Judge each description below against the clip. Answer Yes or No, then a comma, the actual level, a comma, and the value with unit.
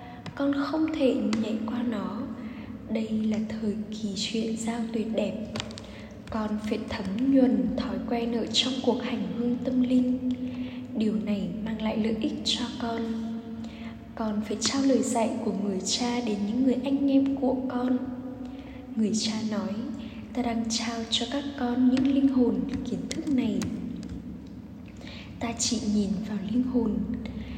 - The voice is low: No, high, 235 Hz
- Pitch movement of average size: No, narrow, 2.3 semitones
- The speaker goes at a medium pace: No, slow, 155 wpm